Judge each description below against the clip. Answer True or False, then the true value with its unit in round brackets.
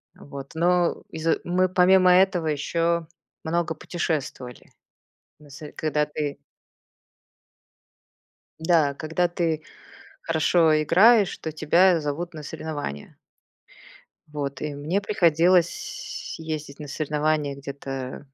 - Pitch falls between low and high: True (160 Hz)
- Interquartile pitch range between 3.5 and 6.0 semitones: False (2.8 semitones)